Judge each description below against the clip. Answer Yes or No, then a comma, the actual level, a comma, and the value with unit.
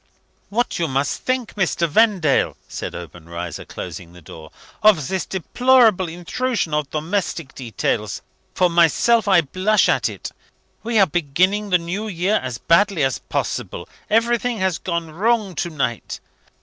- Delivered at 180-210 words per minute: No, average, 145 wpm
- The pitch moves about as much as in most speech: No, wide, 6.0 semitones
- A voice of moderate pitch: Yes, medium, 180 Hz